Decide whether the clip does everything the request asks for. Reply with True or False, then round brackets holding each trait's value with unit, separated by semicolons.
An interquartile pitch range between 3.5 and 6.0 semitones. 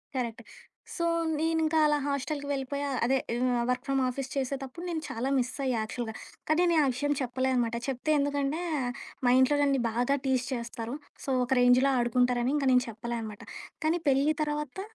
False (2.7 semitones)